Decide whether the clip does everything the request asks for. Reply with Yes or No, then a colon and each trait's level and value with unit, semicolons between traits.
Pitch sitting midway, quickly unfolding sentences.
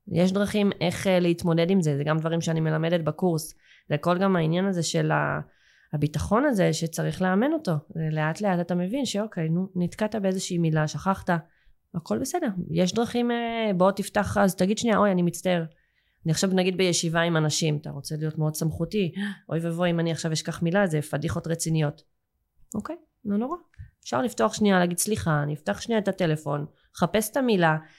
Yes: medium, 175 Hz; fast, 175 wpm